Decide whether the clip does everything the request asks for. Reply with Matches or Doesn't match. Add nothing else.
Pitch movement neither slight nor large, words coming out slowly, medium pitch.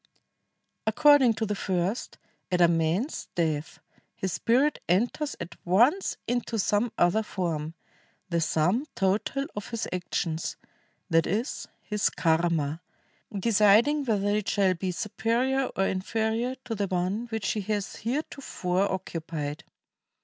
Doesn't match